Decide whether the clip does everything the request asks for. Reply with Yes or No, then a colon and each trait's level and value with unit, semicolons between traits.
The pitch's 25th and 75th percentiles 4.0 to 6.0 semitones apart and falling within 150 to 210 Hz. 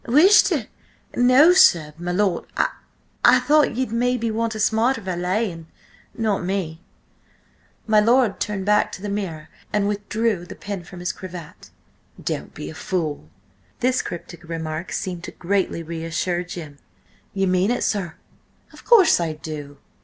Yes: average, 4.8 semitones; high, 190 Hz